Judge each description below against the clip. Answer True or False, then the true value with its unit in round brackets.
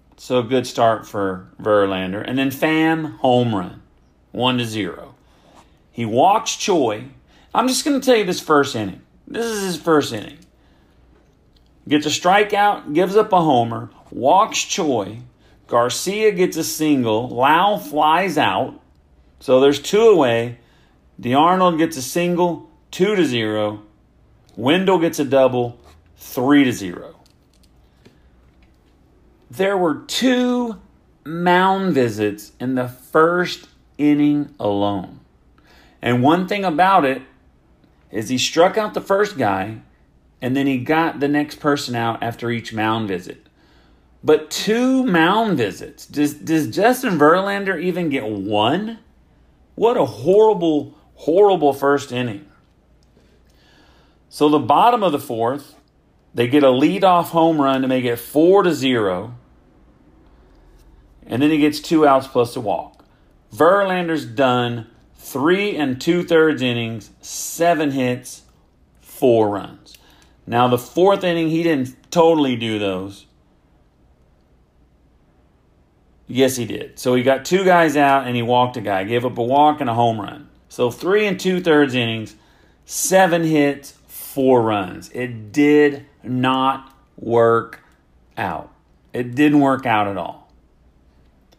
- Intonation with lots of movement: True (7.5 semitones)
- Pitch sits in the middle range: False (130 Hz)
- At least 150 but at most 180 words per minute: False (135 wpm)